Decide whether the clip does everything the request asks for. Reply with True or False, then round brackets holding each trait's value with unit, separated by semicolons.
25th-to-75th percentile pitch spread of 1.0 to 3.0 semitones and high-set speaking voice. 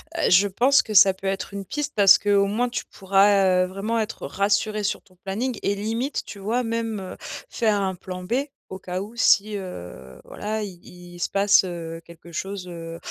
True (2.7 semitones; 200 Hz)